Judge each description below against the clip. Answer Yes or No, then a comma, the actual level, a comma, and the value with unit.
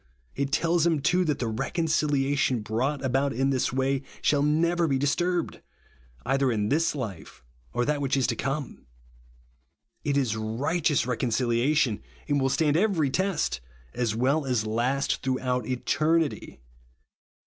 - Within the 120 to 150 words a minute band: Yes, average, 140 wpm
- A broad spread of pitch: No, average, 3.6 semitones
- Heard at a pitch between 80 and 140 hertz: Yes, low, 135 Hz